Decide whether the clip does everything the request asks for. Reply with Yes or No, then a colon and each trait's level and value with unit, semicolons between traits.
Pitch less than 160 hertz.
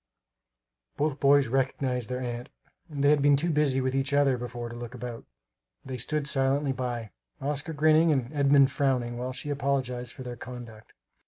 Yes: low, 135 Hz